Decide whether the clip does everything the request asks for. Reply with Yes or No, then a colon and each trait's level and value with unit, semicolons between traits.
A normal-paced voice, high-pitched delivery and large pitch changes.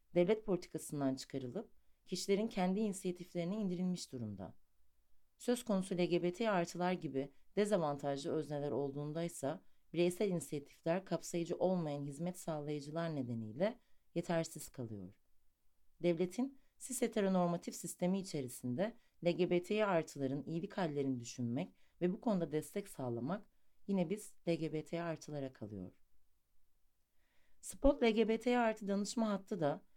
No: average, 105 wpm; medium, 170 Hz; wide, 6.1 semitones